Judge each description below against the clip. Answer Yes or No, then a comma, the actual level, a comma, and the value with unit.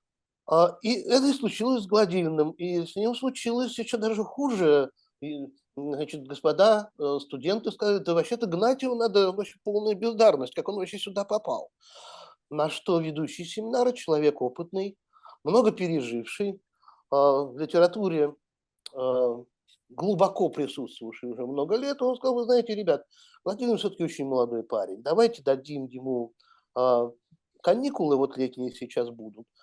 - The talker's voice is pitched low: No, medium, 175 Hz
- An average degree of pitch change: No, wide, 7.7 semitones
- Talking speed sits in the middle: Yes, average, 130 wpm